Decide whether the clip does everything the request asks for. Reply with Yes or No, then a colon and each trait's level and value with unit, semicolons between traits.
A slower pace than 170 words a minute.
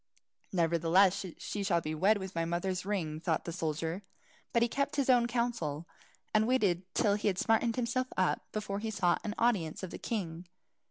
No: average, 195 wpm